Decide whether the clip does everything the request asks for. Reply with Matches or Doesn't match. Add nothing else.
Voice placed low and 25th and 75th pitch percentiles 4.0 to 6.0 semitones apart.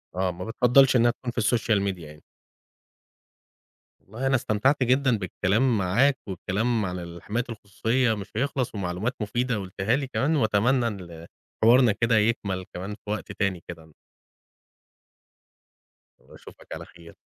Matches